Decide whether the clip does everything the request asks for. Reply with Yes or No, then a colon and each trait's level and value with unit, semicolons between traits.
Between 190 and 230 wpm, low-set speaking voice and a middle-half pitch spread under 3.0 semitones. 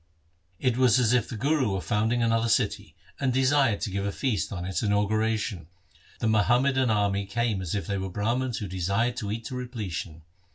No: average, 195 wpm; low, 110 Hz; average, 3.6 semitones